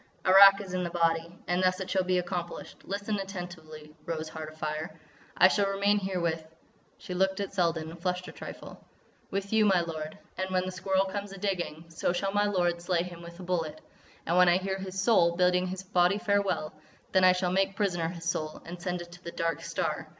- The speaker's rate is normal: No, fast, 215 wpm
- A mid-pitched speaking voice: Yes, medium, 180 Hz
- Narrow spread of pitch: Yes, narrow, 2.2 semitones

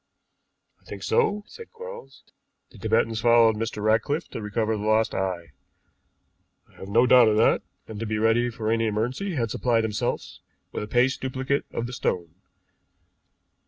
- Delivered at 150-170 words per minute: Yes, average, 165 wpm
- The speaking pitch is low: Yes, low, 115 Hz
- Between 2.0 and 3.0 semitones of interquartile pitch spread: Yes, average, 2.7 semitones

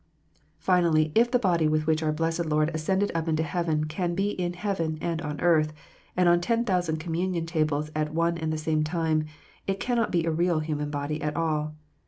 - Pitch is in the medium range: Yes, medium, 160 Hz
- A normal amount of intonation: No, narrow, 2.3 semitones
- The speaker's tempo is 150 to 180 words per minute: No, fast, 205 wpm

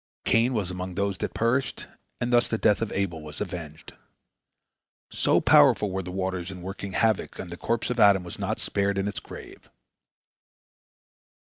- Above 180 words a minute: No, average, 175 wpm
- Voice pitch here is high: No, low, 100 Hz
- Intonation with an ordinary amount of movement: Yes, average, 3.3 semitones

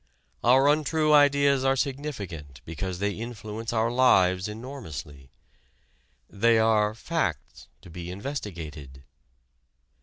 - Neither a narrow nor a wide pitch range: No, wide, 7.1 semitones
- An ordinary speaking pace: No, slow, 100 wpm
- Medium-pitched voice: No, low, 110 Hz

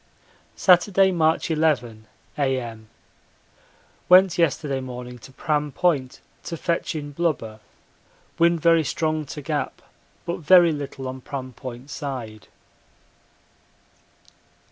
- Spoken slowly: Yes, slow, 105 wpm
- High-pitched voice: No, medium, 145 Hz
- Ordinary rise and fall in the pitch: Yes, average, 4.4 semitones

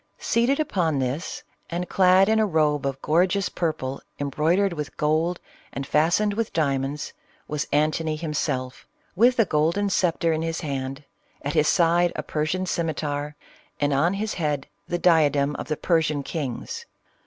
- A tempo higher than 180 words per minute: No, average, 155 wpm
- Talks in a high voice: No, medium, 160 Hz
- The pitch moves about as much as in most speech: Yes, average, 3.5 semitones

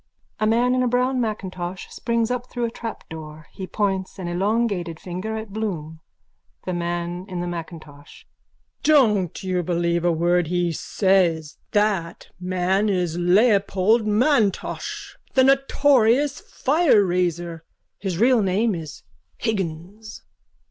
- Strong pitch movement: No, average, 4.4 semitones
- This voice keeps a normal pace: No, slow, 130 wpm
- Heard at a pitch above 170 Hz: Yes, high, 190 Hz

